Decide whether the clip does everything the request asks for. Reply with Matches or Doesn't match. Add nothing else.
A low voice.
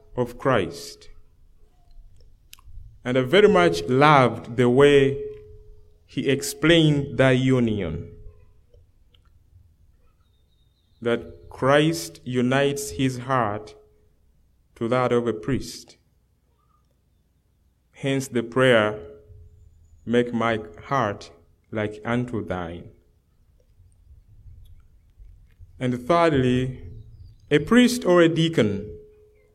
Matches